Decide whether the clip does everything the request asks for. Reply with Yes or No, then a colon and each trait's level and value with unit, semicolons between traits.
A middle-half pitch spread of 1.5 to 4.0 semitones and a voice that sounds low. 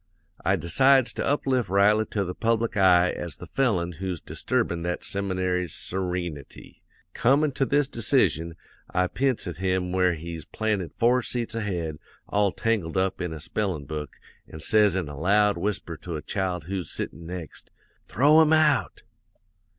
No: average, 4.6 semitones; very low, 95 Hz